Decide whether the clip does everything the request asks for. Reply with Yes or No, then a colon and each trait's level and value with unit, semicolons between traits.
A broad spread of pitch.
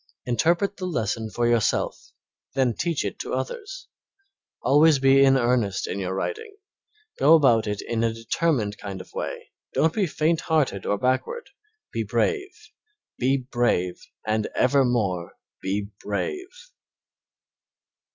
Yes: wide, 7.1 semitones